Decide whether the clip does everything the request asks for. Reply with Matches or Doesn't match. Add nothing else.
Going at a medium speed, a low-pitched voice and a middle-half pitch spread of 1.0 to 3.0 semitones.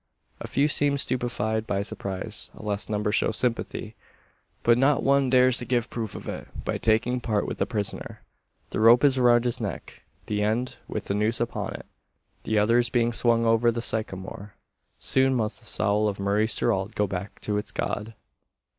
Matches